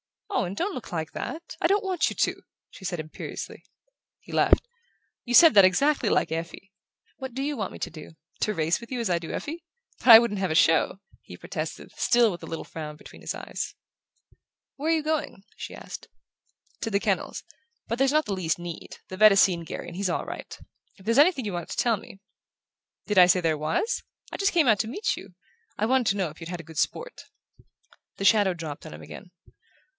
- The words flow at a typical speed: No, fast, 225 wpm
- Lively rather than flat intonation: Yes, wide, 7.3 semitones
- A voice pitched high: Yes, high, 200 Hz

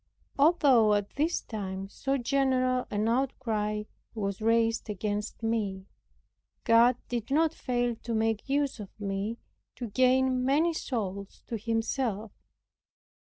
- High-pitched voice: Yes, high, 230 Hz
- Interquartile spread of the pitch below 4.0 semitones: Yes, average, 3.6 semitones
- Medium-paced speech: No, slow, 120 wpm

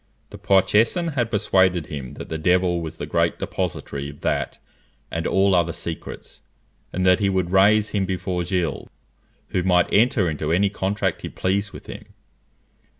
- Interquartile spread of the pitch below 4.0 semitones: Yes, average, 2.7 semitones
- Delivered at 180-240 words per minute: No, average, 165 wpm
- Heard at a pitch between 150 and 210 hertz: No, very low, 95 Hz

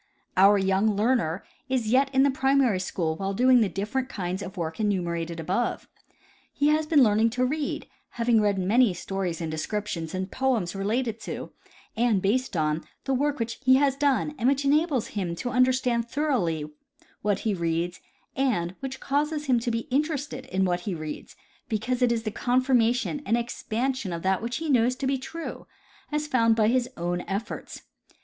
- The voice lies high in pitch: Yes, high, 230 Hz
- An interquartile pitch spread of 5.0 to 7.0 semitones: Yes, wide, 5.5 semitones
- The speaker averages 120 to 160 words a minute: No, average, 180 wpm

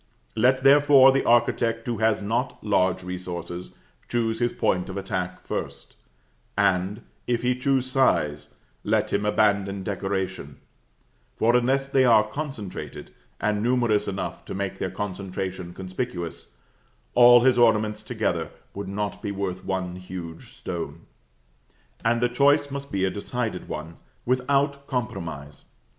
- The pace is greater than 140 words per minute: No, slow, 135 wpm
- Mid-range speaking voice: No, low, 105 Hz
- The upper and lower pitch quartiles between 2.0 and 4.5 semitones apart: No, average, 4.9 semitones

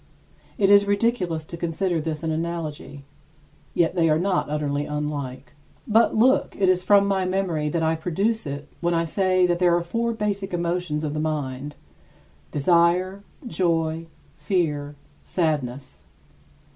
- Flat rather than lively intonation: No, average, 3.8 semitones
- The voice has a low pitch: No, medium, 170 Hz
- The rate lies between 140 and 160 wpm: Yes, average, 150 wpm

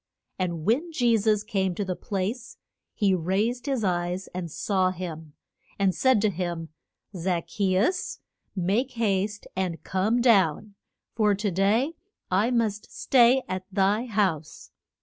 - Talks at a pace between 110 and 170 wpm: Yes, average, 145 wpm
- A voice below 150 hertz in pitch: No, high, 195 Hz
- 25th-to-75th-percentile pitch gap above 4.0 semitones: No, average, 3.6 semitones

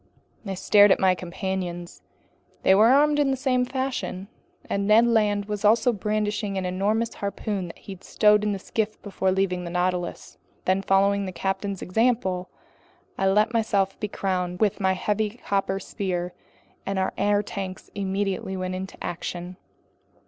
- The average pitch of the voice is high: Yes, high, 195 Hz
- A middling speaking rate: Yes, average, 160 wpm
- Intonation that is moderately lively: No, narrow, 2.1 semitones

